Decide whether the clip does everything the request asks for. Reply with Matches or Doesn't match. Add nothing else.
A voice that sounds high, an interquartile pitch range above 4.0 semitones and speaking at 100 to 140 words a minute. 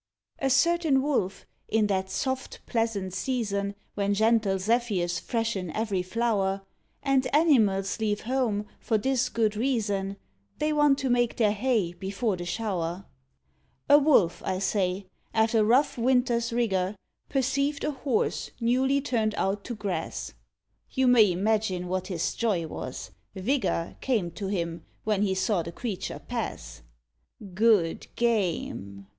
Matches